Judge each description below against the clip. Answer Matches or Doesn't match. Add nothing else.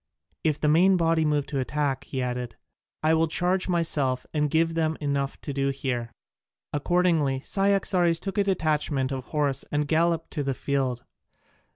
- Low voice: Doesn't match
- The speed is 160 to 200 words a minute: Matches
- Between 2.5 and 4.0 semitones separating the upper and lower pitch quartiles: Matches